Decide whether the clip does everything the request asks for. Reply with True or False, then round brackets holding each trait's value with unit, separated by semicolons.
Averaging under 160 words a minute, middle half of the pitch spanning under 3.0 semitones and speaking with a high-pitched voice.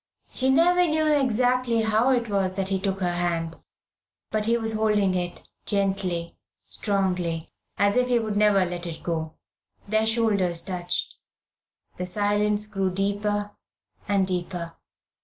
False (140 wpm; 3.5 semitones; 200 Hz)